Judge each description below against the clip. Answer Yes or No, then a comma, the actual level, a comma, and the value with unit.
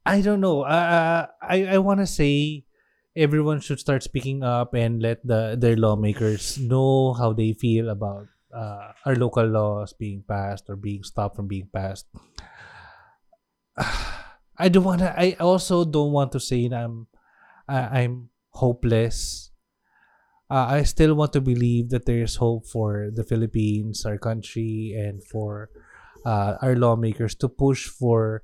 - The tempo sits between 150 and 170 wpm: Yes, fast, 155 wpm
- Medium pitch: No, low, 115 Hz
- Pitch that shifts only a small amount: No, average, 4.5 semitones